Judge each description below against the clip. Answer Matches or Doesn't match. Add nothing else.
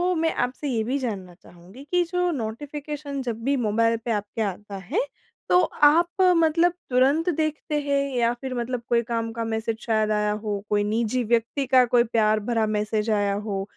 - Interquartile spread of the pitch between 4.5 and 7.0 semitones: Matches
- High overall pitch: Matches